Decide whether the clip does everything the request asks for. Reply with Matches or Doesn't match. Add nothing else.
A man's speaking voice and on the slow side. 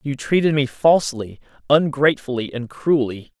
Matches